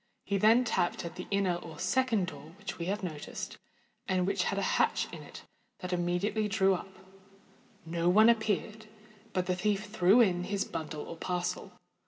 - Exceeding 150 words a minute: Yes, average, 175 wpm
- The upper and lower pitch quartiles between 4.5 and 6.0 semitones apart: No, average, 3.2 semitones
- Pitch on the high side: Yes, high, 195 Hz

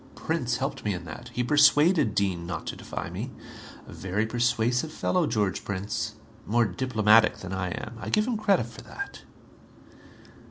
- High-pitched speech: No, low, 115 Hz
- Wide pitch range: Yes, wide, 5.8 semitones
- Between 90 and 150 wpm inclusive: No, average, 165 wpm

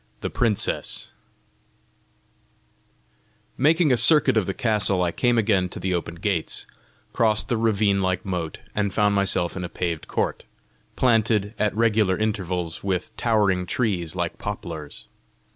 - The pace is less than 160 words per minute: Yes, average, 140 wpm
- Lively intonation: No, average, 3.5 semitones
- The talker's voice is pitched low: Yes, low, 100 Hz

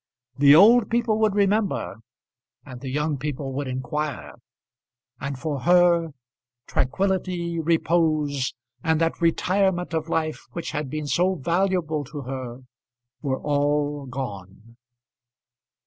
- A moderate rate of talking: No, slow, 115 wpm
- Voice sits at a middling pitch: Yes, medium, 155 Hz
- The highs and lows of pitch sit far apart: No, average, 4.2 semitones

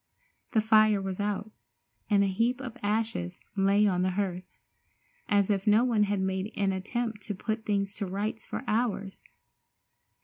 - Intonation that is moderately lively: No, narrow, 2.1 semitones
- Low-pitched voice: No, high, 205 Hz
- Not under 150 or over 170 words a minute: Yes, average, 165 wpm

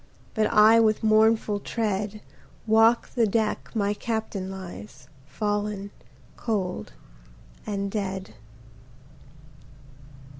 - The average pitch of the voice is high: Yes, high, 210 Hz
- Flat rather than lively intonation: Yes, narrow, 2.1 semitones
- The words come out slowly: Yes, slow, 85 wpm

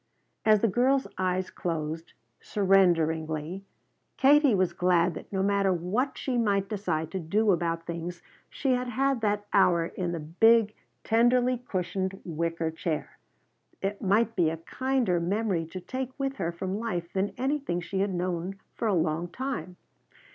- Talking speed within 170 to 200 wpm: No, average, 155 wpm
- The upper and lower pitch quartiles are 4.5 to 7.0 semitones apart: Yes, average, 4.8 semitones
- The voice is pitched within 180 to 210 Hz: Yes, high, 190 Hz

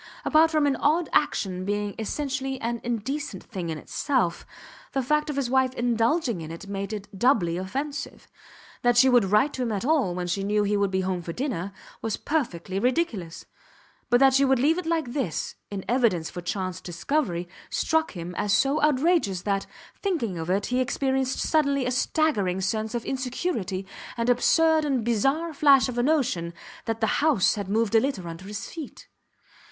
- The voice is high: Yes, high, 240 Hz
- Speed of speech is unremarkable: Yes, average, 185 wpm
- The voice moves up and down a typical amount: No, wide, 6.3 semitones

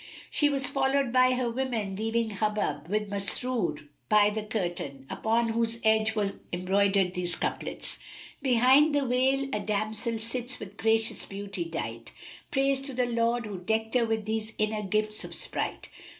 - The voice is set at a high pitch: Yes, high, 220 Hz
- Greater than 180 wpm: No, average, 165 wpm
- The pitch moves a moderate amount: Yes, average, 3.5 semitones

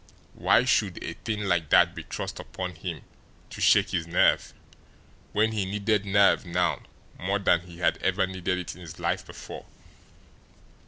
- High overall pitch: No, very low, 95 Hz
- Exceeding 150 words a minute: Yes, average, 165 wpm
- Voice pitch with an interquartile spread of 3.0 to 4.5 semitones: No, narrow, 2.5 semitones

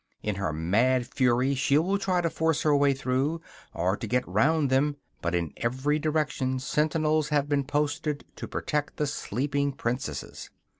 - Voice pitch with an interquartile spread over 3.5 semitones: No, average, 3.2 semitones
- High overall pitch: No, medium, 140 Hz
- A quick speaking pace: No, average, 165 wpm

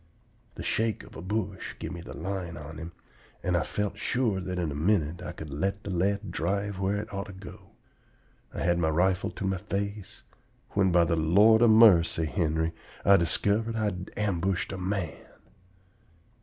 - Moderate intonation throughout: Yes, average, 3.1 semitones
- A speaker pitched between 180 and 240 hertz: No, very low, 95 Hz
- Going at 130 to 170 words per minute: No, average, 185 wpm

